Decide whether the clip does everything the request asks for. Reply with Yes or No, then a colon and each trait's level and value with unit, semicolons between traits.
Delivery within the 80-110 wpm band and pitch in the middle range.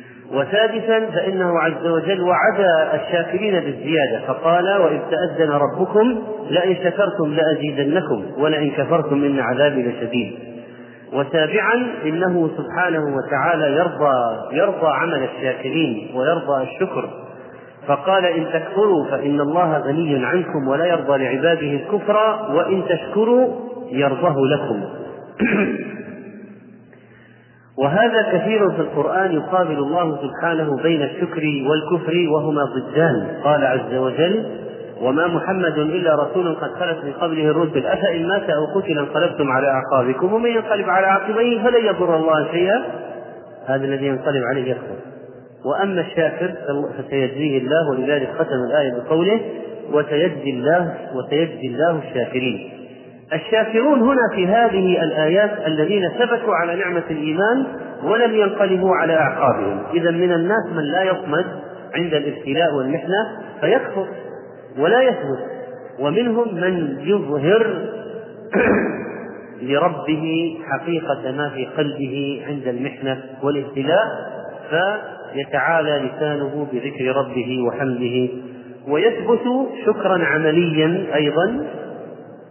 Yes: average, 105 wpm; medium, 160 Hz